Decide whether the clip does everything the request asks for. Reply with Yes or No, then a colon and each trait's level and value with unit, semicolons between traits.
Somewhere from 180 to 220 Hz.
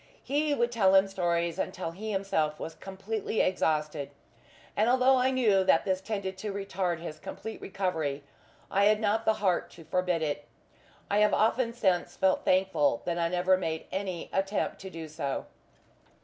Yes: high, 190 Hz